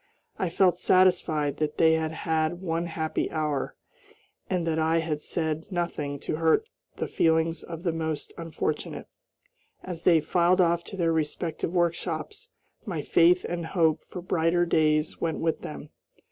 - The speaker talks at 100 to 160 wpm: Yes, average, 155 wpm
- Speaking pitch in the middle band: Yes, medium, 165 Hz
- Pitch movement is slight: Yes, narrow, 1.7 semitones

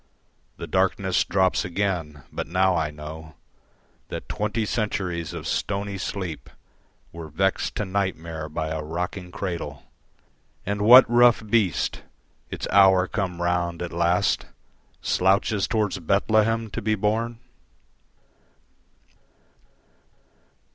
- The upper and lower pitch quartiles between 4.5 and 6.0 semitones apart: No, average, 3.4 semitones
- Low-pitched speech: Yes, very low, 95 Hz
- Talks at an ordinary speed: No, slow, 110 wpm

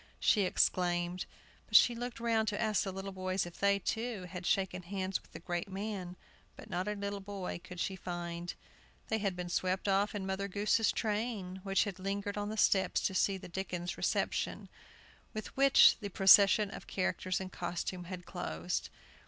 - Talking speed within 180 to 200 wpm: Yes, average, 185 wpm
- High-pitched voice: Yes, high, 195 Hz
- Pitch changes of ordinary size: No, narrow, 2.2 semitones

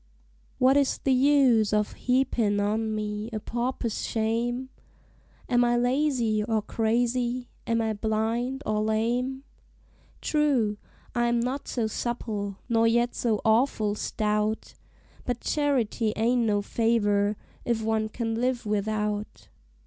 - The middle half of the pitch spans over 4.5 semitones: No, narrow, 2.4 semitones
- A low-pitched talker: No, high, 230 Hz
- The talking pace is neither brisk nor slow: No, slow, 125 wpm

